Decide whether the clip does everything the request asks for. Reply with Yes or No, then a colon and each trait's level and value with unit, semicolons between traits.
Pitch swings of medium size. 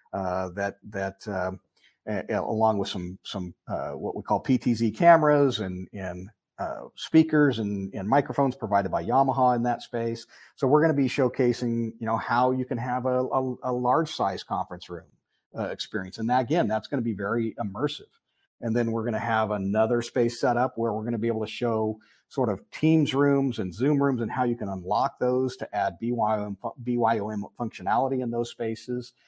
Yes: average, 3.4 semitones